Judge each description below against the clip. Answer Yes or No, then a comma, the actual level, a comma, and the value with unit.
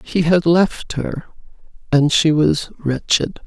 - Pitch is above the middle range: No, medium, 160 Hz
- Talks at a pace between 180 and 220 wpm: No, average, 140 wpm